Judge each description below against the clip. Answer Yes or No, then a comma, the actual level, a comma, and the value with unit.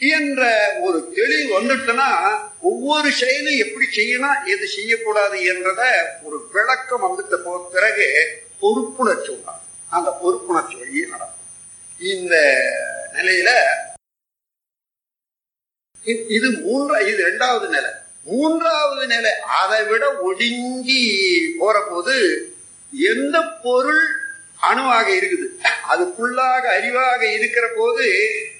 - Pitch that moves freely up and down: Yes, wide, 8.0 semitones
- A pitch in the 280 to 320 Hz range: Yes, very high, 295 Hz